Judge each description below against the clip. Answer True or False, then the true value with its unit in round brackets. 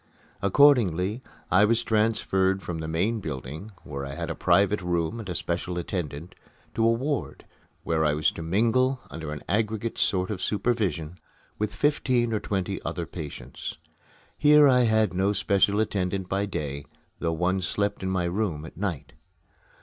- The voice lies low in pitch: True (95 Hz)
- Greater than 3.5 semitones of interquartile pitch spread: True (4.7 semitones)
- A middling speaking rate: True (165 wpm)